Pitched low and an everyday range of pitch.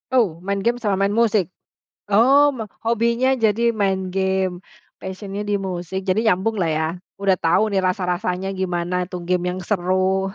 No: high, 195 Hz; average, 3.1 semitones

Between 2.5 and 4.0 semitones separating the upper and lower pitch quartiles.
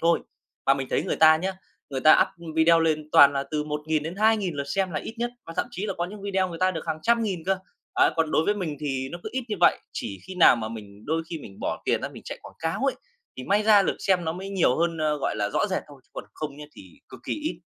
No: average, 4.4 semitones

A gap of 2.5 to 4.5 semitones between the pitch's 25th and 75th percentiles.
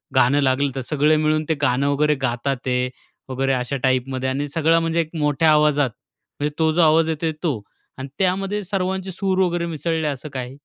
Yes: average, 3.7 semitones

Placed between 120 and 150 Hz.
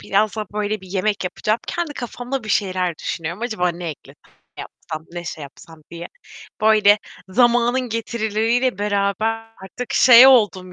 No: high, 215 Hz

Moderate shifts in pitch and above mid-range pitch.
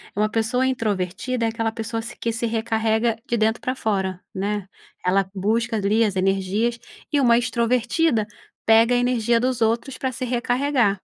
No: narrow, 2.3 semitones; high, 225 Hz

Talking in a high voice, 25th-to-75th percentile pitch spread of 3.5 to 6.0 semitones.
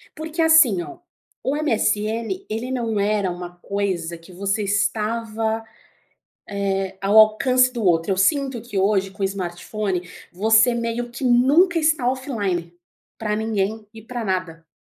Yes: high, 215 Hz; average, 4.0 semitones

